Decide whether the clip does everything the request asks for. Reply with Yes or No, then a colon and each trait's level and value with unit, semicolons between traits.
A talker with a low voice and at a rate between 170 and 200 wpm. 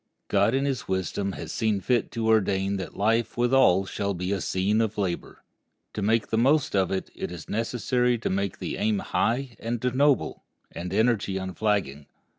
Yes: low, 105 Hz; average, 190 wpm